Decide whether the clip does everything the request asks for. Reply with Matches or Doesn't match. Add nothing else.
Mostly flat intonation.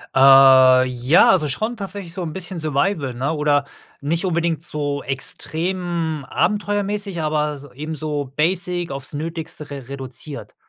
Doesn't match